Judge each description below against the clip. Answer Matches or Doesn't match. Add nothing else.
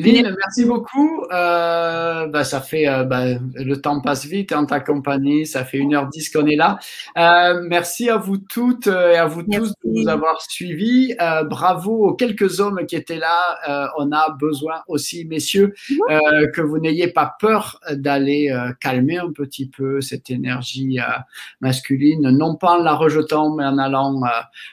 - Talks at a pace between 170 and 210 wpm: Matches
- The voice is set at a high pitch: Doesn't match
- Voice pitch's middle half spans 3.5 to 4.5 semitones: Matches